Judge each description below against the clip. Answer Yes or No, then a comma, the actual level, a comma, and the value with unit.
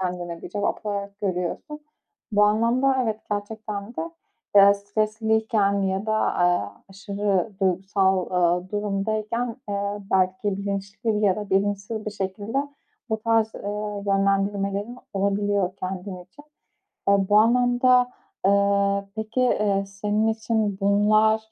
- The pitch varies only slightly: Yes, narrow, 1.8 semitones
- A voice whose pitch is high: Yes, high, 205 Hz